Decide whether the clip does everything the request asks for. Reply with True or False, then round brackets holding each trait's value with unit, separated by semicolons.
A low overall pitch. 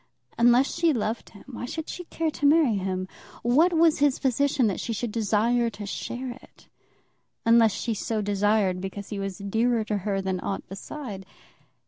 False (225 Hz)